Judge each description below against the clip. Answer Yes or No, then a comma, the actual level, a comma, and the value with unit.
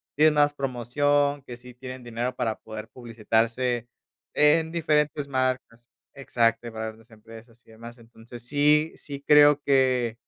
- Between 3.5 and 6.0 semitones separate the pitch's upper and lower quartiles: Yes, average, 3.8 semitones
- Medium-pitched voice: No, low, 125 Hz